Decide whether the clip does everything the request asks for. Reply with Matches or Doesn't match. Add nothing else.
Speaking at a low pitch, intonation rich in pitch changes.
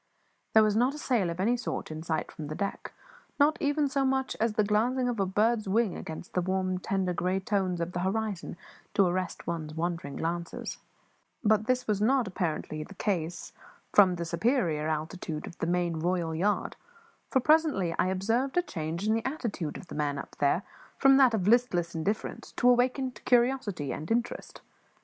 Doesn't match